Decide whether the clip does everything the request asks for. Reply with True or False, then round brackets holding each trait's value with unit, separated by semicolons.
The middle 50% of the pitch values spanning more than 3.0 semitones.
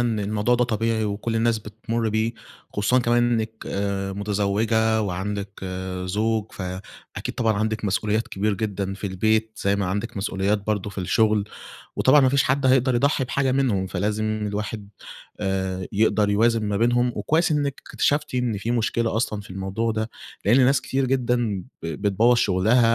False (2.7 semitones)